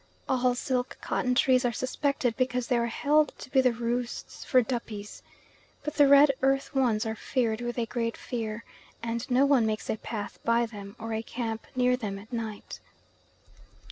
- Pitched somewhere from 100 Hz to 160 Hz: No, high, 240 Hz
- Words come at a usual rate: Yes, average, 180 wpm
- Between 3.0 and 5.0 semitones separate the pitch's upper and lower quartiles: No, narrow, 2.4 semitones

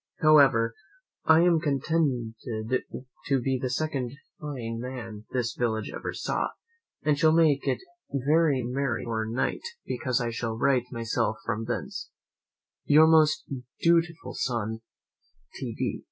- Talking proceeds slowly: Yes, slow, 130 wpm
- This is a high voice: No, low, 130 Hz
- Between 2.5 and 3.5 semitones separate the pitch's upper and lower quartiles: No, average, 4.8 semitones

